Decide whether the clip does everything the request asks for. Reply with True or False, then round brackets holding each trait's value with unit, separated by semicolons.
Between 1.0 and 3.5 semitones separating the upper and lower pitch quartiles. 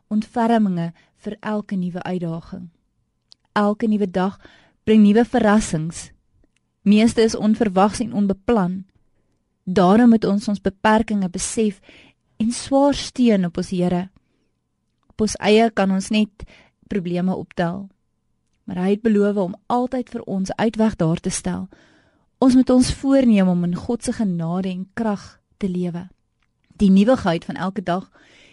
True (3.2 semitones)